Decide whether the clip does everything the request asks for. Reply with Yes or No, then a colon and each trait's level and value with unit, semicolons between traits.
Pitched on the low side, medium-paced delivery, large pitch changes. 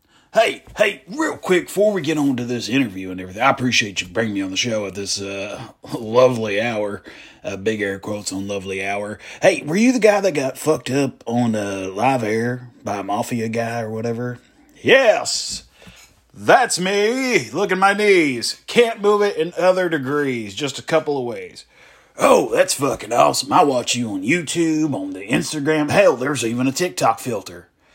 Yes: low, 130 Hz; average, 190 wpm; wide, 9.0 semitones